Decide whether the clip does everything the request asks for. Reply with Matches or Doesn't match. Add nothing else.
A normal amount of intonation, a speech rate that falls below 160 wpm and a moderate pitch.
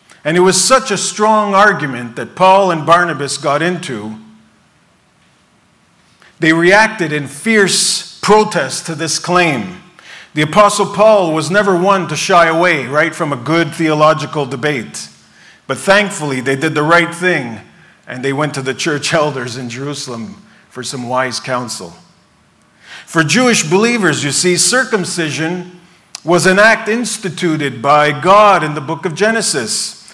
Matches